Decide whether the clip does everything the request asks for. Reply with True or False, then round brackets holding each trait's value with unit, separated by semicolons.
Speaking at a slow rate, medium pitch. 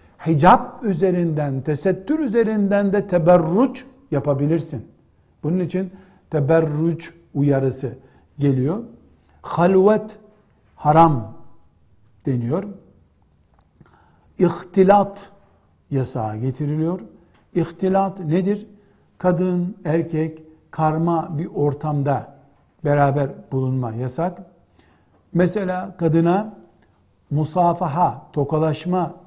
True (65 wpm; 165 Hz)